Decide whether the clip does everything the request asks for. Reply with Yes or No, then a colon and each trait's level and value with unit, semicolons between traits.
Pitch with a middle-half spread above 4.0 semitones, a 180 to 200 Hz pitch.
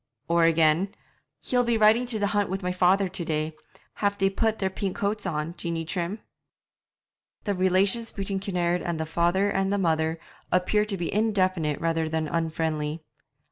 No: average, 3.6 semitones; medium, 185 Hz